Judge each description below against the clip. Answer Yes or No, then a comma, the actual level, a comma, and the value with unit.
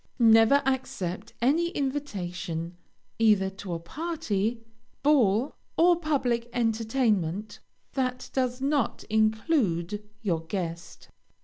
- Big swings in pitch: Yes, wide, 5.9 semitones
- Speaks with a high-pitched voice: Yes, high, 225 Hz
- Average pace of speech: No, slow, 95 wpm